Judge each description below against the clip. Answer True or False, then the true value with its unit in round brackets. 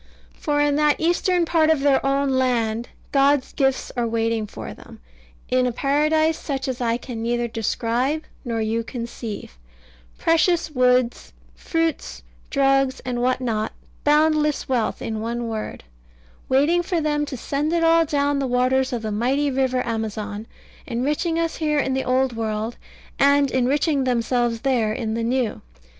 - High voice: True (260 Hz)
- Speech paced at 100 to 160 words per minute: True (155 wpm)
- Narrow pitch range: False (4.0 semitones)